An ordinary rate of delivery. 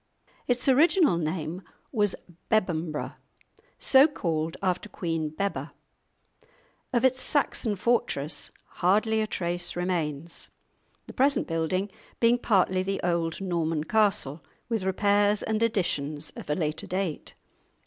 No: slow, 120 wpm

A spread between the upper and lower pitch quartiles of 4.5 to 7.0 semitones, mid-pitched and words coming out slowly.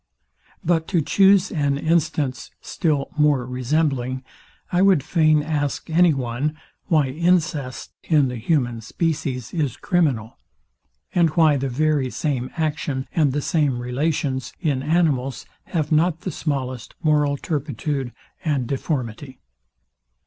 No: average, 3.5 semitones; medium, 145 Hz; slow, 125 wpm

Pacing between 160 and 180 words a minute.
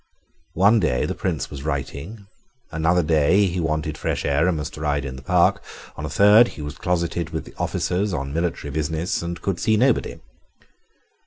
Yes: average, 175 wpm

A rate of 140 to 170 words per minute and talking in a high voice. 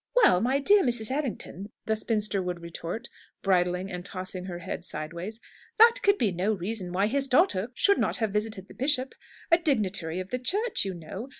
No: average, 190 wpm; high, 210 Hz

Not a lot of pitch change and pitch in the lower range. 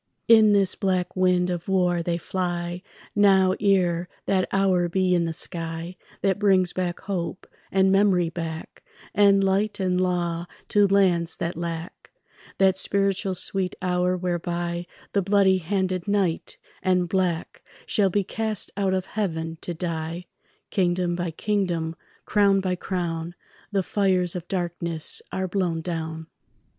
No: narrow, 2.1 semitones; medium, 180 Hz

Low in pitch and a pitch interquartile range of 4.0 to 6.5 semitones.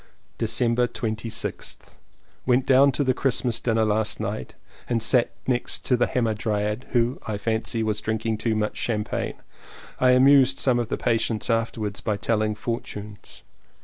No: low, 115 Hz; narrow, 2.4 semitones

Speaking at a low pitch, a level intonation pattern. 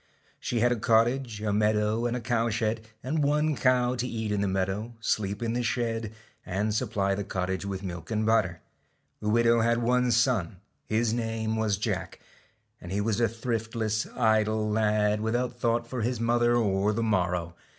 Yes: low, 110 Hz; narrow, 2.2 semitones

